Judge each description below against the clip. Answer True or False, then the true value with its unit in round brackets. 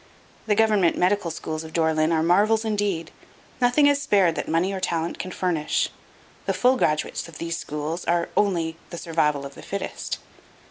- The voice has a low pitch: False (170 Hz)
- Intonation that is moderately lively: True (4.1 semitones)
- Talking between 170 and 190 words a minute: True (180 wpm)